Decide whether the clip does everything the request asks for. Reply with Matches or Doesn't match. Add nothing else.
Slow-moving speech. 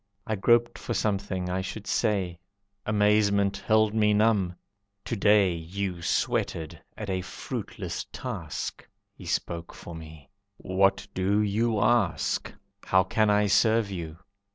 Matches